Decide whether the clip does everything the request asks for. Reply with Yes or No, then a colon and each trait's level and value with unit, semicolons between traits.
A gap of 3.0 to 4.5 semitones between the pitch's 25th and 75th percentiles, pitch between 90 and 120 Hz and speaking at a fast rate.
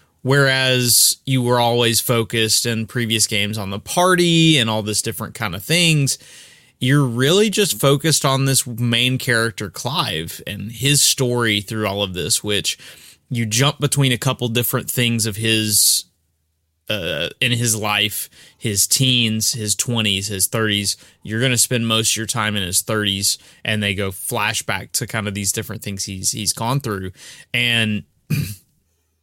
No: average, 3.8 semitones; low, 110 Hz; average, 165 wpm